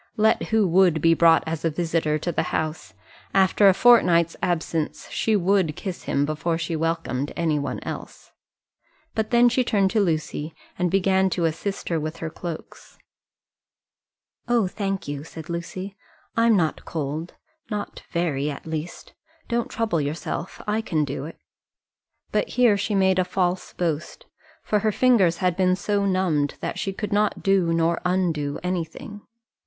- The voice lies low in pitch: No, medium, 175 Hz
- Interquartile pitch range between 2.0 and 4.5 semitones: Yes, average, 3.7 semitones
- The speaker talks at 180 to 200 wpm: No, average, 165 wpm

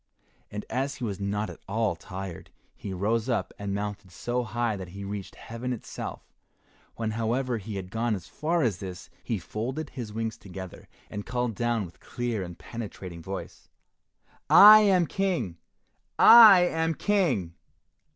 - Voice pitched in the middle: No, low, 110 Hz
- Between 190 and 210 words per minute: No, average, 160 wpm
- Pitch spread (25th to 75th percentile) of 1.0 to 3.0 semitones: No, average, 4.4 semitones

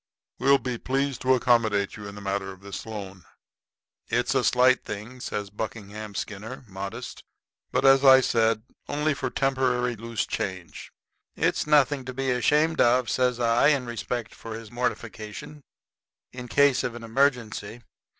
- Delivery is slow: No, average, 155 wpm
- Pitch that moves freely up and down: No, average, 3.5 semitones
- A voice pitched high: No, low, 120 Hz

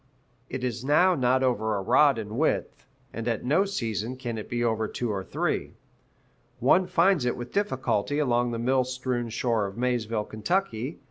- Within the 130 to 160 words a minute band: No, average, 180 wpm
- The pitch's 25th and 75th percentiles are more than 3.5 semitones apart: No, average, 2.9 semitones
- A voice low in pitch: Yes, low, 125 Hz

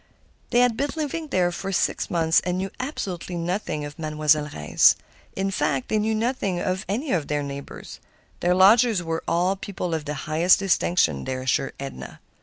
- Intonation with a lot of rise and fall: No, average, 4.7 semitones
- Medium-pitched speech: Yes, medium, 180 Hz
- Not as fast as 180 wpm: No, average, 185 wpm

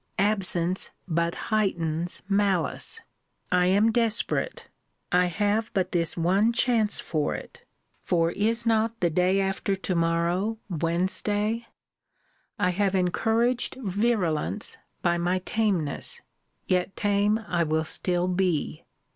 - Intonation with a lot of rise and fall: No, average, 3.8 semitones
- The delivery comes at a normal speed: No, slow, 115 wpm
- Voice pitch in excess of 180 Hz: Yes, high, 190 Hz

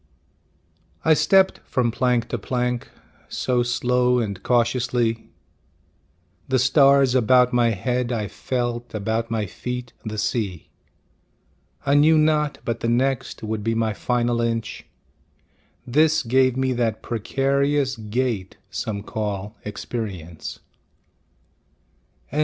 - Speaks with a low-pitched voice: Yes, low, 120 Hz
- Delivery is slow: Yes, slow, 115 wpm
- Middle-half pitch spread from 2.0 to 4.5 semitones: Yes, average, 2.7 semitones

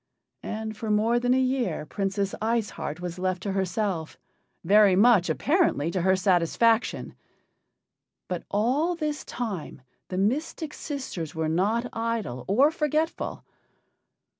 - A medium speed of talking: No, slow, 130 wpm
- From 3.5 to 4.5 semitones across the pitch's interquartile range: No, average, 5.1 semitones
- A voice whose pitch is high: Yes, high, 210 Hz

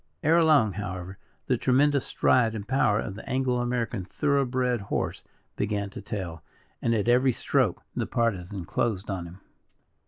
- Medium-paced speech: Yes, average, 160 wpm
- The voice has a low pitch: Yes, low, 115 Hz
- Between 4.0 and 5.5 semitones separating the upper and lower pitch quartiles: Yes, average, 4.6 semitones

